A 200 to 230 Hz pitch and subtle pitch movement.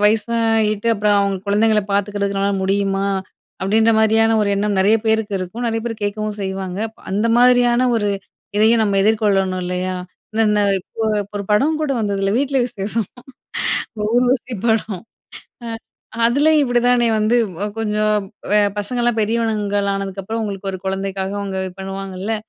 Yes: high, 210 Hz; narrow, 2.3 semitones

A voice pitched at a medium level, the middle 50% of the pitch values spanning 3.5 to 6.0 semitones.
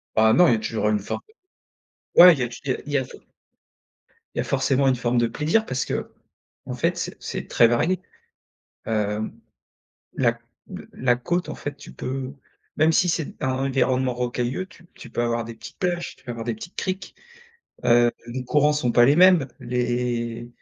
No: low, 125 Hz; average, 4.0 semitones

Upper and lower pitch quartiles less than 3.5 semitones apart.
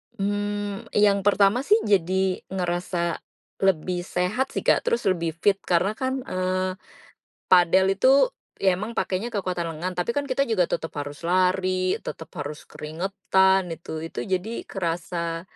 Yes: average, 2.7 semitones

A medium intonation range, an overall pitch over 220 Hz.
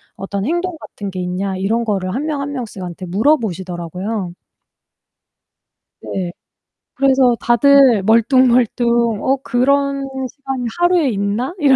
No: wide, 5.9 semitones; high, 235 Hz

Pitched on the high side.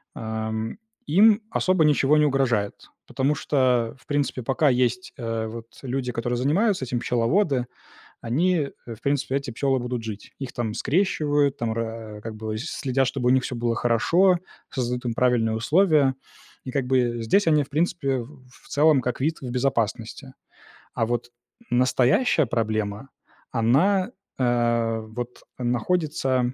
No: low, 125 Hz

